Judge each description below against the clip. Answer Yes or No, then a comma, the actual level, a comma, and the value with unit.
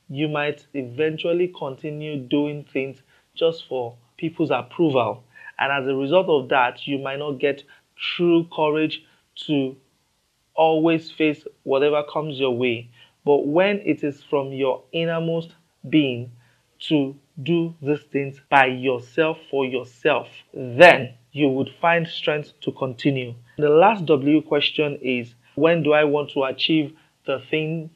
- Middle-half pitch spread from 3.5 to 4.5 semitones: No, average, 2.9 semitones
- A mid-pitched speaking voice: Yes, medium, 145 Hz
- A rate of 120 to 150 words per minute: Yes, average, 140 wpm